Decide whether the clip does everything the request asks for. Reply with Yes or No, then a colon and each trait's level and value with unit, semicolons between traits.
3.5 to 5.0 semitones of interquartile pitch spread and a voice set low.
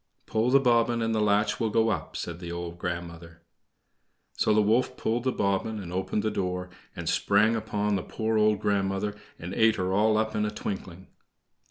No: average, 3.0 semitones; low, 105 Hz